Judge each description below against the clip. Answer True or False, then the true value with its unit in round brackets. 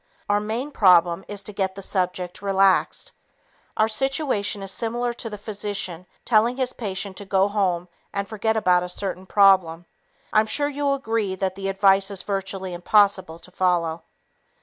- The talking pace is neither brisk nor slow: True (165 wpm)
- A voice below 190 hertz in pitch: False (195 Hz)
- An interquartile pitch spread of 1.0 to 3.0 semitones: True (2.6 semitones)